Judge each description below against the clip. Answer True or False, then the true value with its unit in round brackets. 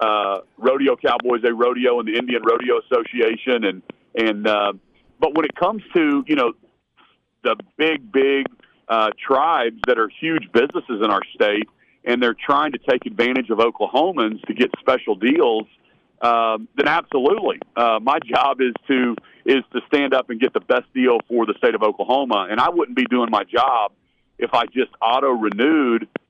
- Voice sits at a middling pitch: False (125 Hz)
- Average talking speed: True (180 wpm)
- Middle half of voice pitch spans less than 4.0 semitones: False (5.5 semitones)